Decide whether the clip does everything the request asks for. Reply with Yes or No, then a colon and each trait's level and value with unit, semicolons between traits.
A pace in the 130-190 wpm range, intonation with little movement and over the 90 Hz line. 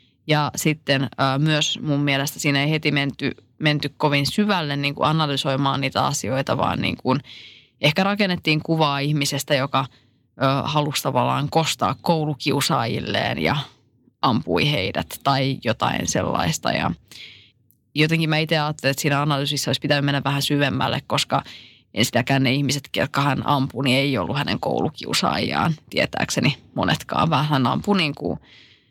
Yes: average, 140 wpm; narrow, 2.1 semitones; medium, 140 Hz